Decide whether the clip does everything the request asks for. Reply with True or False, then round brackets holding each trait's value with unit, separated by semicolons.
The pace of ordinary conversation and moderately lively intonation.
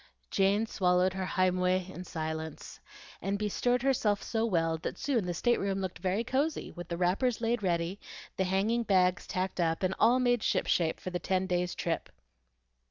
True (175 wpm; 3.7 semitones)